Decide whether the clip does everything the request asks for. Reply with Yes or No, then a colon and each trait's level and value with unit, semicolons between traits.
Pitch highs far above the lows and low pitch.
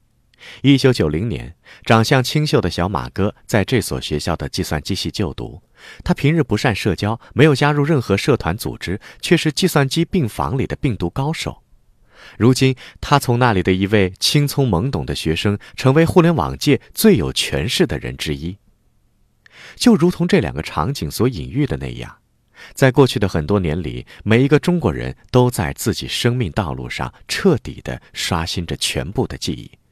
Yes: wide, 8.8 semitones; low, 115 Hz